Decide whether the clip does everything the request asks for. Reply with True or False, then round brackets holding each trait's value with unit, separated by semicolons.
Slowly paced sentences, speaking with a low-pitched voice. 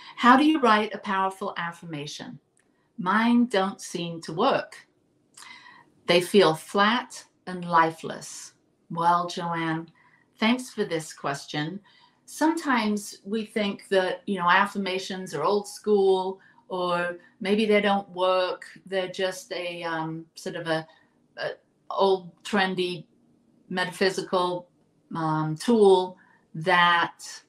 False (115 wpm; 190 Hz)